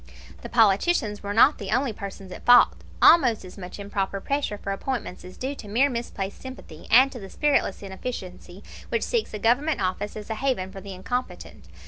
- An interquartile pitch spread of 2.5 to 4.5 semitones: No, average, 5.0 semitones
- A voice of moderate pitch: No, high, 210 Hz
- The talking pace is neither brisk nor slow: Yes, average, 190 wpm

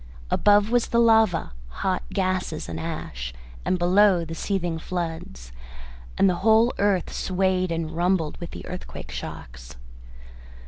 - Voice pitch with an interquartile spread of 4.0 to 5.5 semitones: No, average, 3.4 semitones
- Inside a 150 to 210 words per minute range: No, slow, 135 wpm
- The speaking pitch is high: No, medium, 180 Hz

